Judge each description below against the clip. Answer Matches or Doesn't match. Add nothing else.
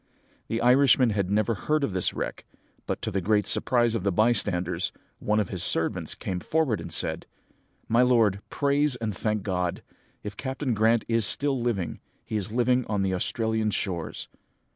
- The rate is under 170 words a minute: Doesn't match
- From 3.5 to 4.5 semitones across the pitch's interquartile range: Matches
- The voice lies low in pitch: Matches